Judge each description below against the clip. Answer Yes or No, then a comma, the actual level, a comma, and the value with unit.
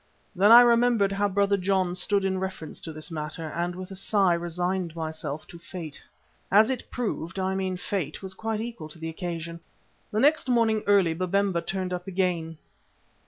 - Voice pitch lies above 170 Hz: Yes, medium, 185 Hz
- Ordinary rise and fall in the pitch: Yes, average, 3.1 semitones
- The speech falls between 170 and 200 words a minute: Yes, average, 190 wpm